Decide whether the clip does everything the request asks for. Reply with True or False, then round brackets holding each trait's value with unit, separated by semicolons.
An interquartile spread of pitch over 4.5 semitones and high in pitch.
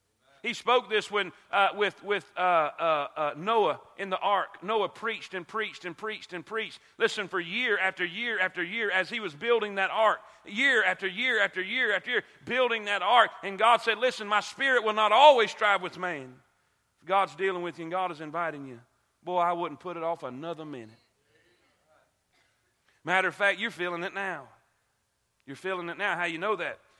False (3.6 semitones; 195 Hz)